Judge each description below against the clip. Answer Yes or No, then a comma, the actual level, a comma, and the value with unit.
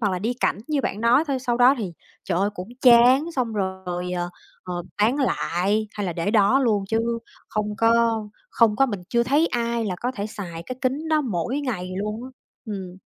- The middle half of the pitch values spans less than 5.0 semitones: Yes, average, 4.6 semitones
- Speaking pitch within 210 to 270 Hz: Yes, high, 220 Hz